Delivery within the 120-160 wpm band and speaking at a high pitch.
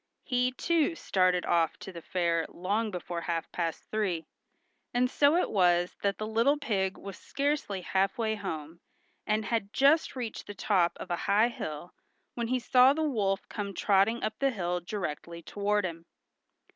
No: average, 170 wpm; high, 200 Hz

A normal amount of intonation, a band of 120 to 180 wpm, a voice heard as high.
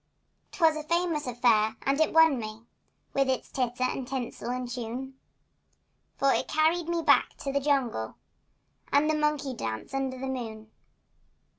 Yes: average, 3.8 semitones; average, 155 wpm; very high, 265 Hz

